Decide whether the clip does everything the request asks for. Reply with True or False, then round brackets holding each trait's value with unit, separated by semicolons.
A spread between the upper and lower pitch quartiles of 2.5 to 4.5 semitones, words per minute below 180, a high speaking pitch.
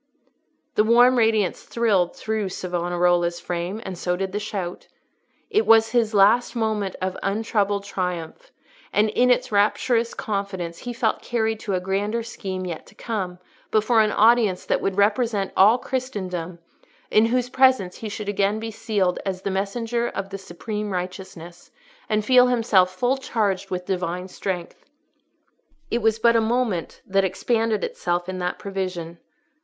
True (3.5 semitones; 155 wpm; 205 Hz)